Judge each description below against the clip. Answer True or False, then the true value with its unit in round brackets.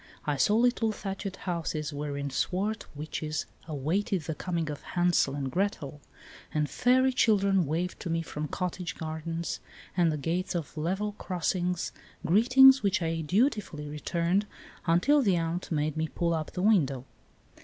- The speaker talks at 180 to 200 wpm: False (150 wpm)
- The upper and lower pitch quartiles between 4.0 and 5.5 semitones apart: True (4.3 semitones)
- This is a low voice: False (170 Hz)